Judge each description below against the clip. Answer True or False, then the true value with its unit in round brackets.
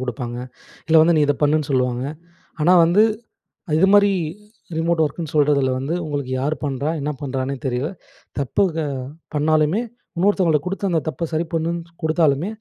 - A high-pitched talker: False (155 Hz)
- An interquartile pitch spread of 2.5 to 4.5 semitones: True (3.3 semitones)